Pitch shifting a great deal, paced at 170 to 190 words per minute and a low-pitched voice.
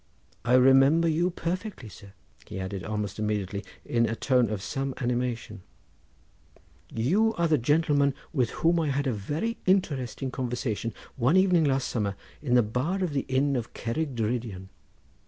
No: wide, 5.7 semitones; average, 155 wpm; low, 130 Hz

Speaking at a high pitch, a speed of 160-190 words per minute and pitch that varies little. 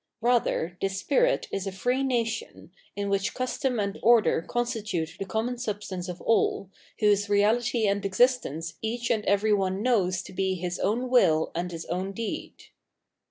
No: high, 205 Hz; average, 165 wpm; average, 4.1 semitones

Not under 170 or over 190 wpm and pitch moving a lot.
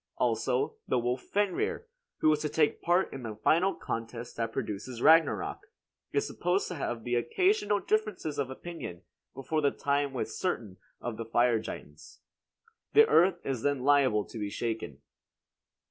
No: average, 155 wpm; wide, 6.9 semitones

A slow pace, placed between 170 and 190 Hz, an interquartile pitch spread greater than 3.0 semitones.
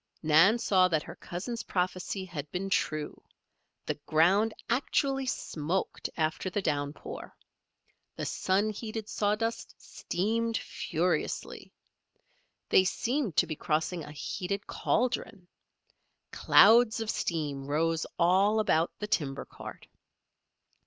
Yes: slow, 110 wpm; medium, 185 Hz; wide, 5.5 semitones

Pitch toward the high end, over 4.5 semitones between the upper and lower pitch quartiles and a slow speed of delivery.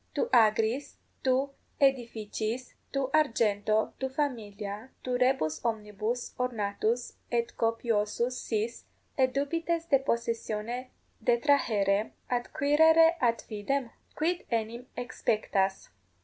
No: high, 235 Hz; average, 3.7 semitones; slow, 95 wpm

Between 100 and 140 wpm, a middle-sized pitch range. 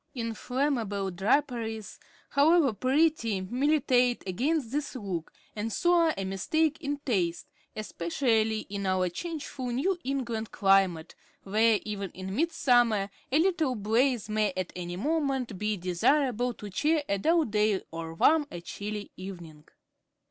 No: slow, 135 wpm; wide, 6.3 semitones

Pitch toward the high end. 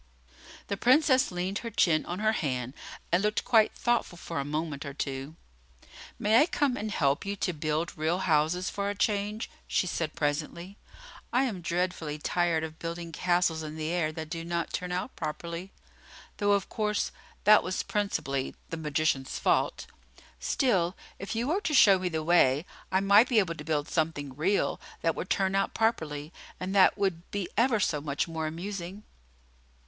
No: medium, 175 Hz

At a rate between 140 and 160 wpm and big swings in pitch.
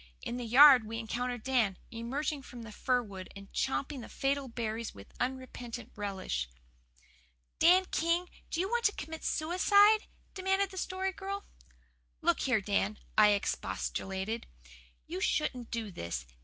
Yes: average, 145 wpm; wide, 7.1 semitones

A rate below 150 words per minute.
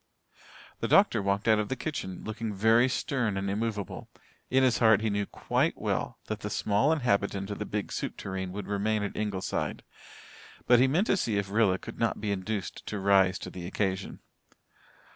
No: average, 190 wpm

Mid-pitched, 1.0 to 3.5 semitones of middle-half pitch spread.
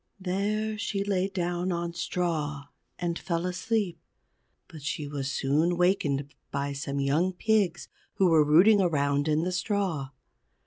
No: medium, 175 Hz; average, 4.5 semitones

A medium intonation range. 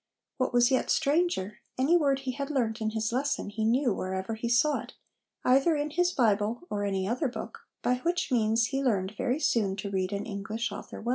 Yes: average, 4.7 semitones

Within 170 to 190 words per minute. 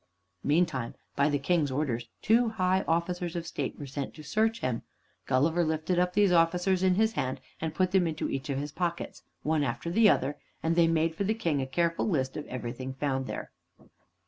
No: average, 200 wpm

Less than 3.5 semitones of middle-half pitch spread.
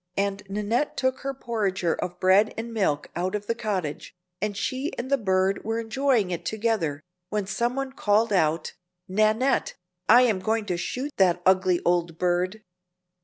No: average, 3.8 semitones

